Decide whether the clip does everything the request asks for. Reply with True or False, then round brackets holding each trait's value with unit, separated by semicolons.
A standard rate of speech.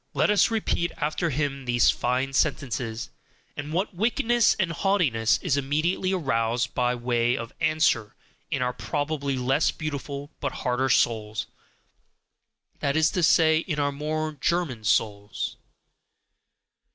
False (130 wpm)